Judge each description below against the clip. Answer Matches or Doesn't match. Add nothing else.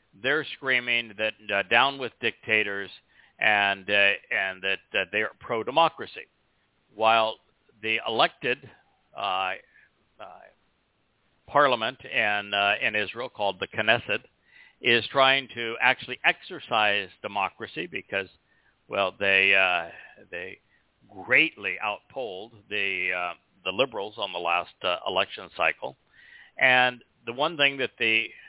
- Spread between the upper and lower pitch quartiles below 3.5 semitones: Matches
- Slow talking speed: Matches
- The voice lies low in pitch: Matches